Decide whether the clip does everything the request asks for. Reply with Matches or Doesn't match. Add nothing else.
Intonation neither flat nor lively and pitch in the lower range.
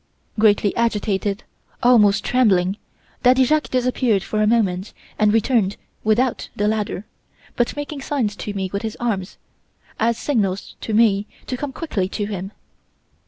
Doesn't match